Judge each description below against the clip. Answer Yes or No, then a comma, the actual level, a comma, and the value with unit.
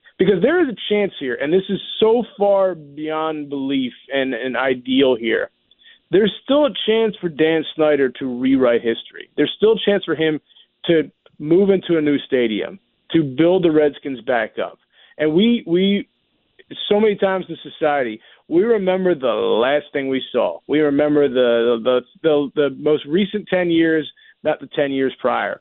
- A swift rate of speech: No, average, 175 wpm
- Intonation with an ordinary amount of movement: No, wide, 6.0 semitones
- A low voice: No, medium, 155 Hz